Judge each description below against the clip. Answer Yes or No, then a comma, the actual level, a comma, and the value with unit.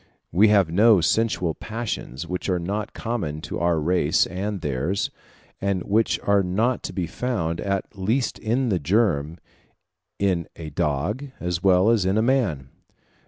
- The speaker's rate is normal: Yes, average, 160 wpm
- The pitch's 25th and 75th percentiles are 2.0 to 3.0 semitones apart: No, average, 4.5 semitones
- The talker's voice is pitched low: Yes, very low, 95 Hz